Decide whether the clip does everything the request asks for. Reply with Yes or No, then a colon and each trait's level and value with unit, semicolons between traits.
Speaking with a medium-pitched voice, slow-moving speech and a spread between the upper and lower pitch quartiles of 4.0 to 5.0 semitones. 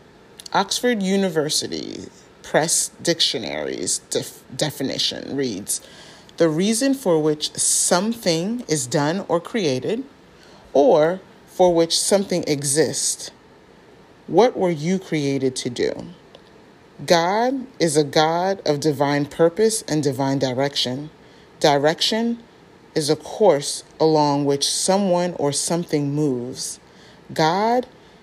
Yes: medium, 165 Hz; slow, 100 wpm; average, 4.4 semitones